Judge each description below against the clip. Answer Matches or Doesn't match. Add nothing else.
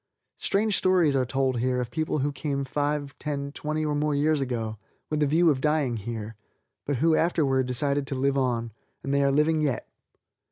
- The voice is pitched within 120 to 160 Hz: Matches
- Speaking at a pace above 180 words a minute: Matches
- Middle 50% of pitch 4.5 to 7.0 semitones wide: Doesn't match